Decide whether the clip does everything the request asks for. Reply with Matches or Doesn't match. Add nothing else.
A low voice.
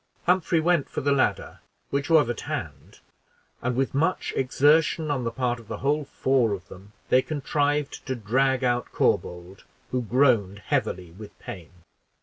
Matches